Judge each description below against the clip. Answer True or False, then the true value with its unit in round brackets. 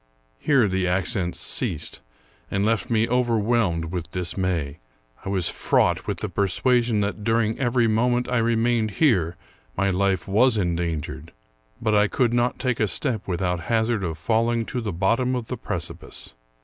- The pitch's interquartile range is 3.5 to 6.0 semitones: True (4.3 semitones)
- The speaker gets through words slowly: False (160 wpm)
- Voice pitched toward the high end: False (110 Hz)